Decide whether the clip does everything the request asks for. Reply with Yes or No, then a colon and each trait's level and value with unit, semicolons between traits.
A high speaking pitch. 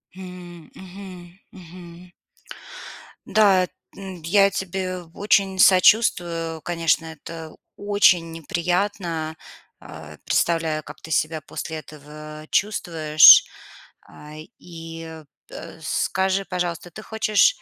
No: medium, 175 Hz